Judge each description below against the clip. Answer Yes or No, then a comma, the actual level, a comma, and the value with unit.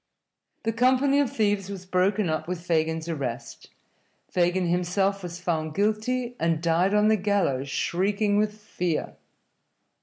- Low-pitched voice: No, medium, 185 Hz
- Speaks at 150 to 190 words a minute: No, average, 140 wpm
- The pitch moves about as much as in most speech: Yes, average, 3.9 semitones